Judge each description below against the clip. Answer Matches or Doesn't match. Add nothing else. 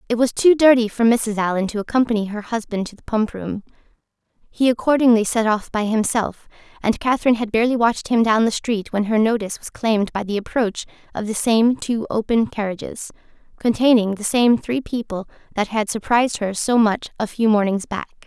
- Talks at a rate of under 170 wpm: Doesn't match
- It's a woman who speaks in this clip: Matches